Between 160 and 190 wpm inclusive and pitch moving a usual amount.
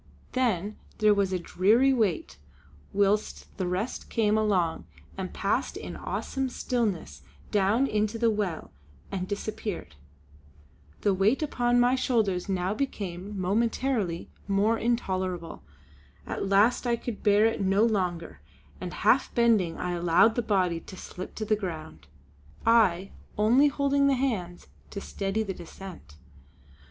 No: slow, 135 wpm; average, 3.9 semitones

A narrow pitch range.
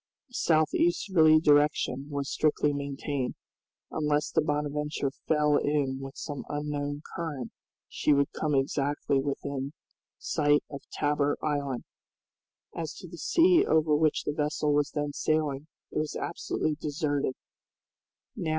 Yes: narrow, 1.4 semitones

